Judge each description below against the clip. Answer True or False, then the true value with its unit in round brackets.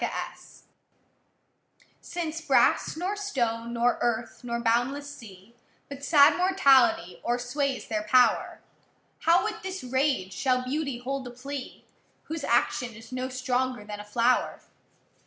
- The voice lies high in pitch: True (255 Hz)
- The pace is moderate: False (130 wpm)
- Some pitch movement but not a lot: True (3.4 semitones)